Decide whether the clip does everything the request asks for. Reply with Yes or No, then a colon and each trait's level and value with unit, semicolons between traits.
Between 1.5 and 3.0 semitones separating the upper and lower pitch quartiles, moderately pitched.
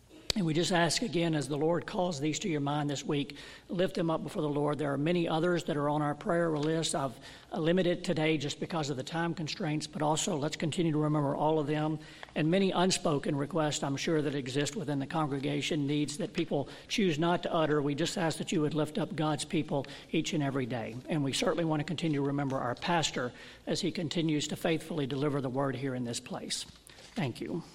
Yes: narrow, 2.5 semitones; medium, 155 Hz